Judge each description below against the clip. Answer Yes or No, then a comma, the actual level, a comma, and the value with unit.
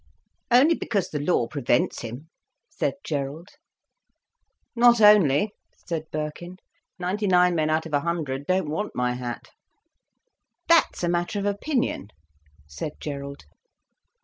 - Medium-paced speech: No, slow, 125 wpm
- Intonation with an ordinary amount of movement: No, wide, 5.9 semitones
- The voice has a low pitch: No, medium, 165 Hz